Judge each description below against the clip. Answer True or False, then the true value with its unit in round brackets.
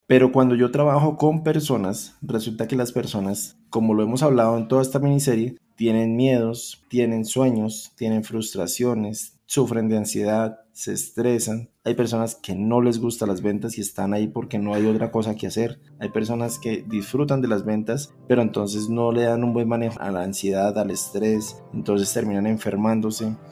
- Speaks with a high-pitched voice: False (115 Hz)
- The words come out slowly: False (180 wpm)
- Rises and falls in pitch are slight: True (2.2 semitones)